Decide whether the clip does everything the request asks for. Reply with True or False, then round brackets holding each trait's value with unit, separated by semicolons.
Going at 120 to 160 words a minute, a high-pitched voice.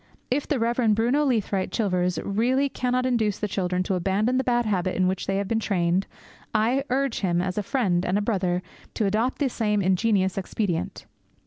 False (195 wpm; 210 Hz)